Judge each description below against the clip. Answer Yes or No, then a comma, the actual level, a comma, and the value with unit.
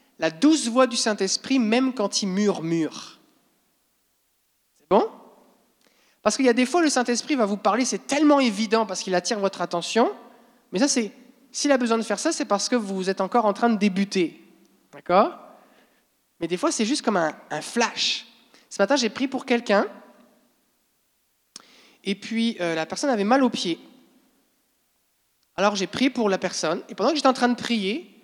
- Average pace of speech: Yes, average, 185 wpm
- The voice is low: No, high, 230 Hz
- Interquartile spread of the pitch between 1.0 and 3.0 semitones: No, average, 4.3 semitones